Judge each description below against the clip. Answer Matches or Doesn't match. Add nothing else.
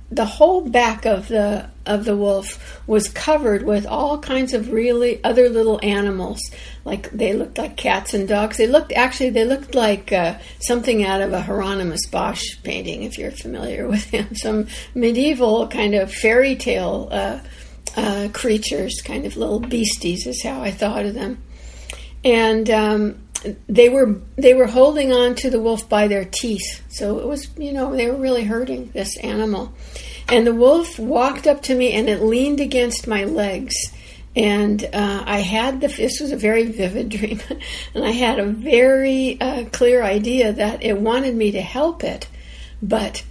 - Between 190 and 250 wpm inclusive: Doesn't match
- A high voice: Matches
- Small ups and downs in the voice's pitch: Doesn't match